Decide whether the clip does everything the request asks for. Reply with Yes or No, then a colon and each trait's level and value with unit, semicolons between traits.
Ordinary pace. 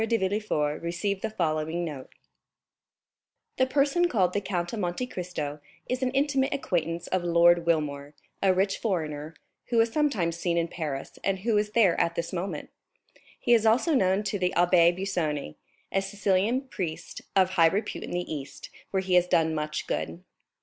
Yes: average, 175 wpm